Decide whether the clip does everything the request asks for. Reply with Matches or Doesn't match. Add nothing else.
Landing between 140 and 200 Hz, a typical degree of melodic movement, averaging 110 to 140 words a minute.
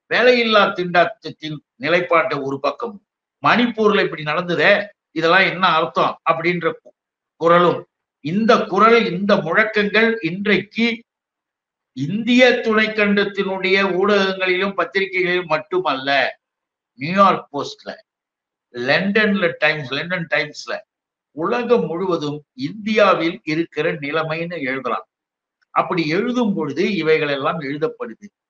Doesn't match